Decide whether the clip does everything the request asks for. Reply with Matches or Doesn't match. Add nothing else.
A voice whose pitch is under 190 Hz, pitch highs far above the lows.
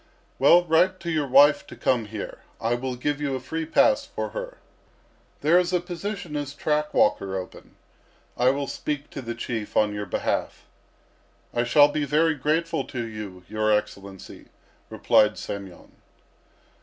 Matches